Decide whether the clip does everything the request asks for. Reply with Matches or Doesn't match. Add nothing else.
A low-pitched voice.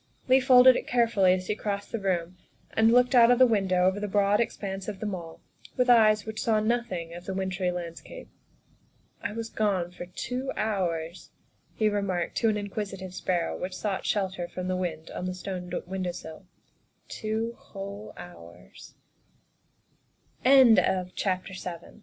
Doesn't match